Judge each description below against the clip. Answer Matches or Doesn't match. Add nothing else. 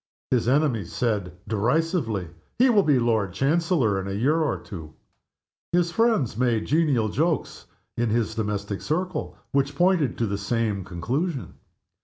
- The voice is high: Doesn't match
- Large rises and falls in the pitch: Matches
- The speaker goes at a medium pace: Matches